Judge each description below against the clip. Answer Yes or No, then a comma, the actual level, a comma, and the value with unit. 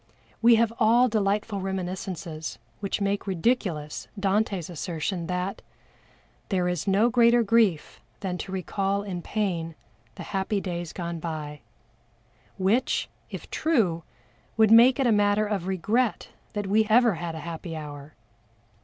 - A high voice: Yes, high, 195 Hz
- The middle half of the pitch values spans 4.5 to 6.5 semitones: No, average, 4.0 semitones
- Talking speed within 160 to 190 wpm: No, slow, 135 wpm